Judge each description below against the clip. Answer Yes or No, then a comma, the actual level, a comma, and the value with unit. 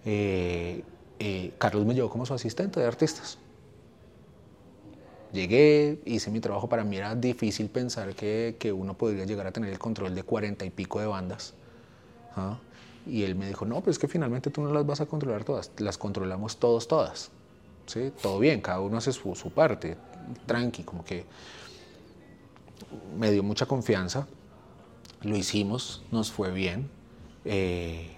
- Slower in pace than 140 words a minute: No, average, 165 wpm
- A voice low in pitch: Yes, low, 110 Hz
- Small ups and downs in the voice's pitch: No, average, 3.6 semitones